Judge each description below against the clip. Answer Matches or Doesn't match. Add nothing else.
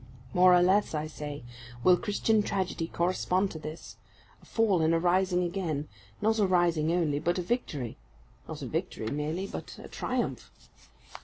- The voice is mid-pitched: Matches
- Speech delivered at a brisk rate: Doesn't match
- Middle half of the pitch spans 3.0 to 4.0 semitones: Matches